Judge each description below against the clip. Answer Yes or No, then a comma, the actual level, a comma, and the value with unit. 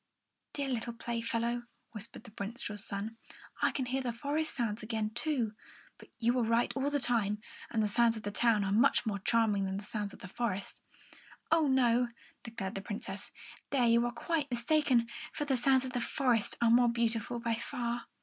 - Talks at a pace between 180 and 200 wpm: Yes, average, 195 wpm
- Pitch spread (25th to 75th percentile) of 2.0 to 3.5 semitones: Yes, narrow, 2.4 semitones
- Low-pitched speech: No, high, 235 Hz